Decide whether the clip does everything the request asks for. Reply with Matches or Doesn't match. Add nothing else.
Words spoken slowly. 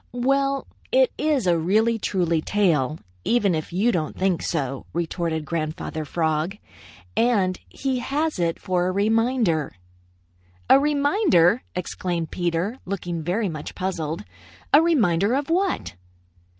Matches